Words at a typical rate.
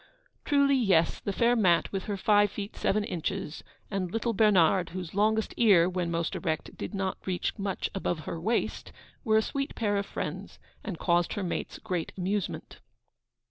Yes: average, 175 wpm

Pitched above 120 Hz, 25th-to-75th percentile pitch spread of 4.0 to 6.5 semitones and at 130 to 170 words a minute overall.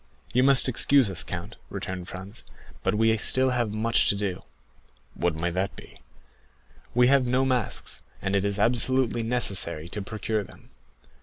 No: low, 110 Hz; average, 4.4 semitones; average, 160 wpm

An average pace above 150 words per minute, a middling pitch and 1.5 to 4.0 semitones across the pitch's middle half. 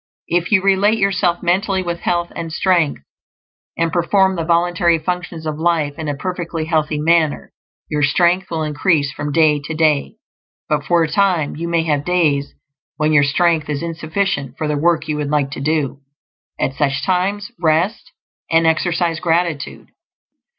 Yes: average, 165 wpm; medium, 165 Hz; narrow, 2.6 semitones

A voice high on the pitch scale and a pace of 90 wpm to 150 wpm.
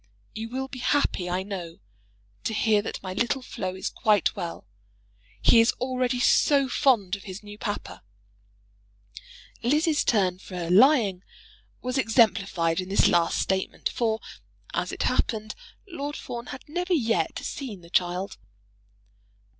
Yes: high, 215 Hz; average, 140 wpm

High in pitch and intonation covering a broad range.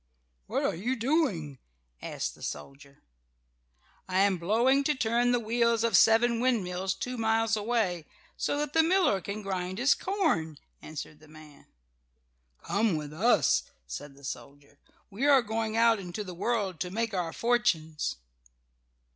Yes: high, 210 Hz; wide, 6.2 semitones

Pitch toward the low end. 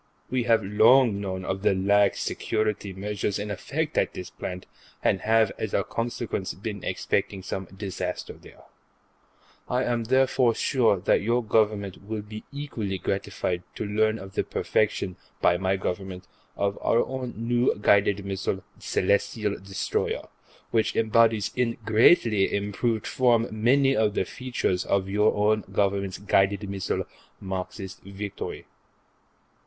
Yes: low, 105 Hz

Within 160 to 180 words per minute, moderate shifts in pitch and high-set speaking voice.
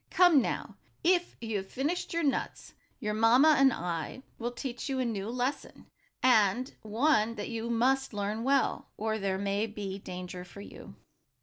Yes: average, 170 wpm; average, 4.7 semitones; high, 230 Hz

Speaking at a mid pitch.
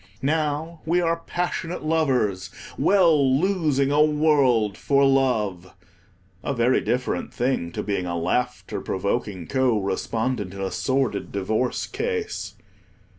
No: low, 130 Hz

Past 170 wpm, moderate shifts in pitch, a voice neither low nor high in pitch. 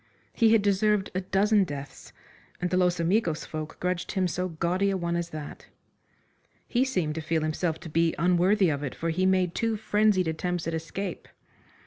Yes: average, 185 wpm; average, 3.1 semitones; medium, 180 Hz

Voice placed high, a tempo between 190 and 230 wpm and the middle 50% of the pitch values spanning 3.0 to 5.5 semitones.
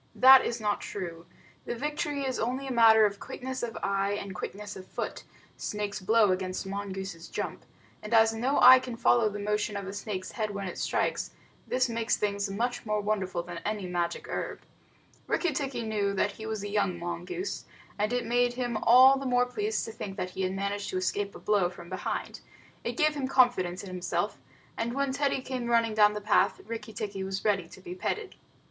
Yes: high, 210 Hz; fast, 205 wpm; average, 4.0 semitones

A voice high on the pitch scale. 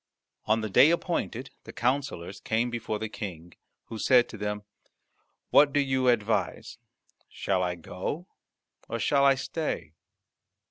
No: low, 115 Hz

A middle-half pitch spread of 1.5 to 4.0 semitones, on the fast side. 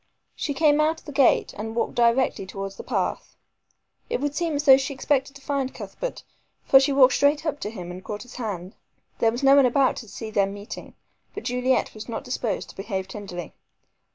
No: average, 5.2 semitones; fast, 210 wpm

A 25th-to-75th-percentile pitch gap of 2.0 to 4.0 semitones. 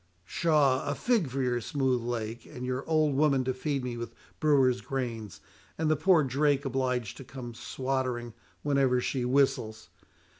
Yes: narrow, 2.6 semitones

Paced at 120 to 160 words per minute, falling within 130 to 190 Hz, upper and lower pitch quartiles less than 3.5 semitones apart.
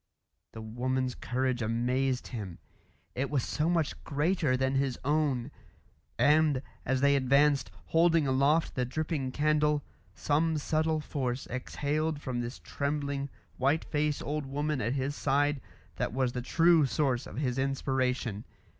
Yes: average, 140 wpm; medium, 140 Hz; average, 2.8 semitones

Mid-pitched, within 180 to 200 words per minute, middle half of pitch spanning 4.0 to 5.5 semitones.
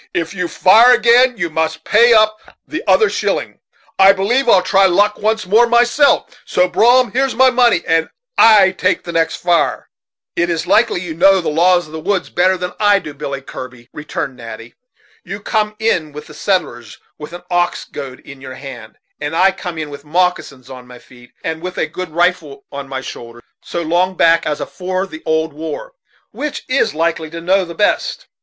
Yes: medium, 175 Hz; average, 195 wpm; average, 5.0 semitones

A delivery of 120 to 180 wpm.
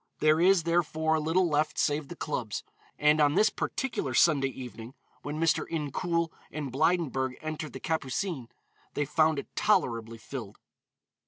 Yes: average, 145 wpm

